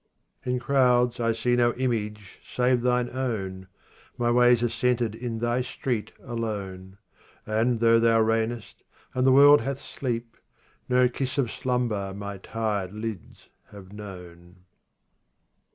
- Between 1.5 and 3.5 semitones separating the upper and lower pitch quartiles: Yes, average, 2.9 semitones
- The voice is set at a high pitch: No, low, 115 Hz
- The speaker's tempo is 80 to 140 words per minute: Yes, slow, 135 wpm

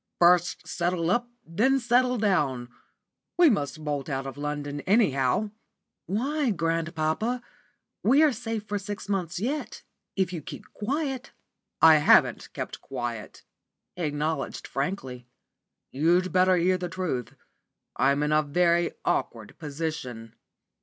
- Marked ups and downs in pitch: Yes, wide, 6.1 semitones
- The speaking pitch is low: No, medium, 170 Hz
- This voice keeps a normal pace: No, slow, 125 wpm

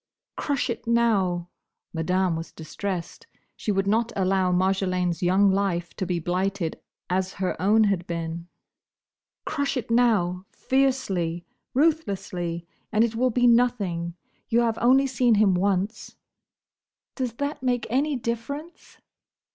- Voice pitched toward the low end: No, high, 200 Hz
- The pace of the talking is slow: Yes, slow, 130 wpm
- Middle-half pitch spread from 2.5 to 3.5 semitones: No, average, 5.0 semitones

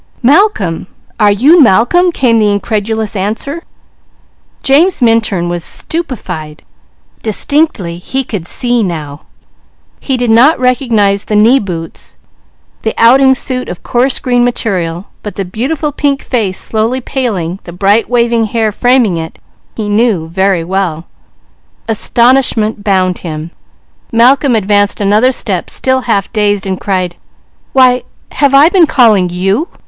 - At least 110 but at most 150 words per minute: Yes, slow, 135 wpm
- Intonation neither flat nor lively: Yes, average, 5.0 semitones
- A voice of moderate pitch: No, high, 220 Hz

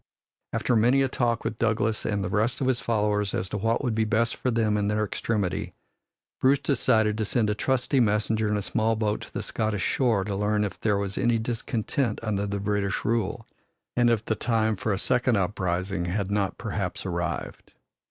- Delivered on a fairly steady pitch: Yes, narrow, 2.2 semitones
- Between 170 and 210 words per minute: Yes, average, 200 wpm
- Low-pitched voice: Yes, low, 110 Hz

